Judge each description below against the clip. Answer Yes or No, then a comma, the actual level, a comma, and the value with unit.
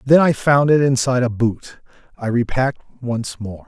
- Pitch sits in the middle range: No, low, 125 Hz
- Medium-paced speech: Yes, average, 180 wpm